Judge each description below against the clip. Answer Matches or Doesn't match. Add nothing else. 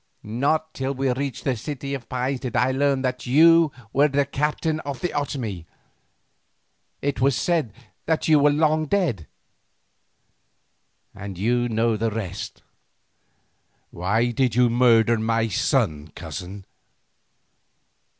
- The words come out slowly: Matches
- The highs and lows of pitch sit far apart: Doesn't match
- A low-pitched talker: Matches